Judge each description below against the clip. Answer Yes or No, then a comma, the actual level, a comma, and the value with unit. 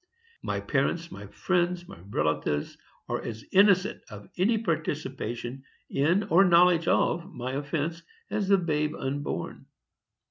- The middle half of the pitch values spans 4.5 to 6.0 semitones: Yes, wide, 5.5 semitones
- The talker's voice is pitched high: No, medium, 160 Hz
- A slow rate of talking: Yes, slow, 130 wpm